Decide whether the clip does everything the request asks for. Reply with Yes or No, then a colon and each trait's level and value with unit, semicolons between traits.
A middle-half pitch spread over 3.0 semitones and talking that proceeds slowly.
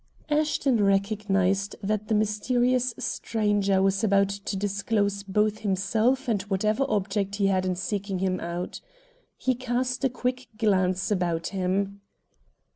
No: narrow, 2.4 semitones; slow, 130 wpm